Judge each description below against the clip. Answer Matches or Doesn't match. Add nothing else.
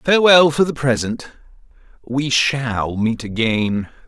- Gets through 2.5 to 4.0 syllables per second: Matches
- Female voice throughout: Doesn't match